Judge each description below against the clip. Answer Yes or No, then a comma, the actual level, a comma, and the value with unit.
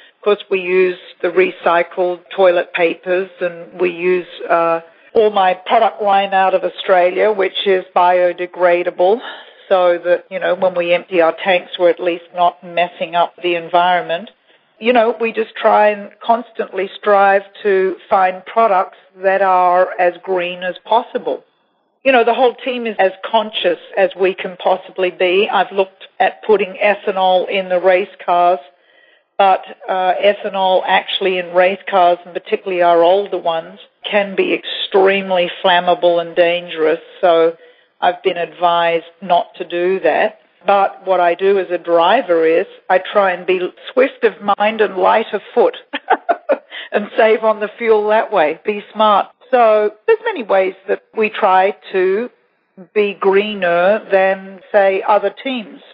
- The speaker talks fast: No, average, 155 wpm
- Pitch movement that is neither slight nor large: Yes, average, 3.2 semitones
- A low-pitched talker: No, high, 190 Hz